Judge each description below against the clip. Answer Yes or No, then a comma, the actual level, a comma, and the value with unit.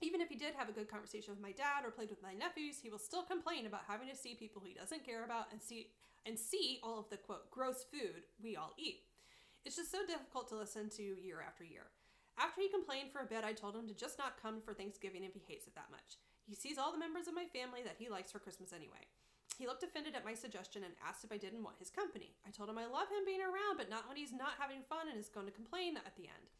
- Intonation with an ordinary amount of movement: No, wide, 7.0 semitones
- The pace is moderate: No, fast, 280 wpm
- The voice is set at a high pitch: Yes, high, 240 Hz